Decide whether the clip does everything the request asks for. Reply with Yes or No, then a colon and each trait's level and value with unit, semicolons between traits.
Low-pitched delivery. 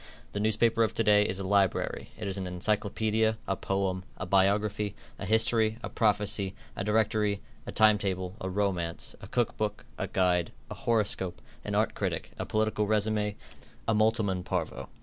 Yes: low, 105 Hz